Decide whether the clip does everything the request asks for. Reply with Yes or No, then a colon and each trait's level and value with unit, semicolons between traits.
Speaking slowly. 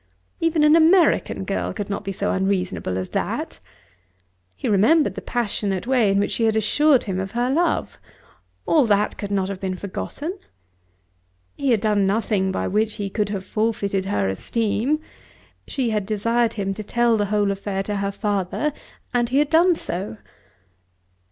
No: average, 170 wpm